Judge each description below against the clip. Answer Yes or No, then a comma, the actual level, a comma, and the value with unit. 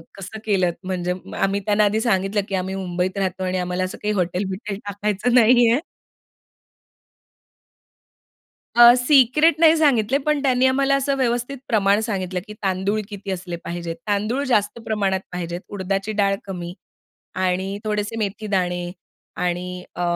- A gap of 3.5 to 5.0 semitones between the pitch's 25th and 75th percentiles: Yes, average, 4.0 semitones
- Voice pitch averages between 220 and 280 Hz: No, high, 200 Hz